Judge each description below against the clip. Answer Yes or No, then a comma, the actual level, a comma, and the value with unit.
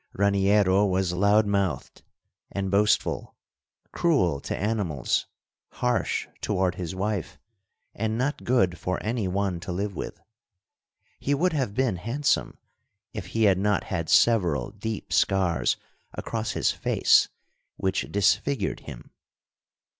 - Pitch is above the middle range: No, low, 100 Hz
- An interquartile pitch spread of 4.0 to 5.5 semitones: No, average, 3.2 semitones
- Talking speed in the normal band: No, slow, 125 wpm